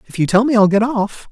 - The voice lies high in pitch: Yes, high, 220 Hz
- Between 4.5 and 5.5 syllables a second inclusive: No, 6.0 syllables/s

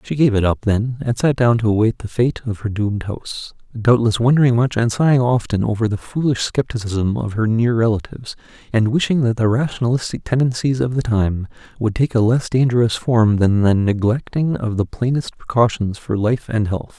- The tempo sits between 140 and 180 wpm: No, average, 200 wpm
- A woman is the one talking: No, male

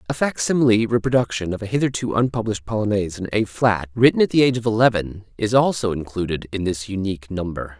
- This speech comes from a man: Yes, male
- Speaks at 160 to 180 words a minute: No, average, 190 wpm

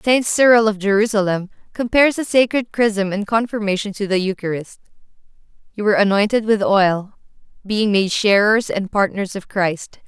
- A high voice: Yes, high, 205 Hz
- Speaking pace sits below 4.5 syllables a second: No, 5.0 syllables/s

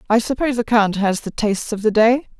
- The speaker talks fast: Yes, fast, 250 wpm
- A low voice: No, high, 225 Hz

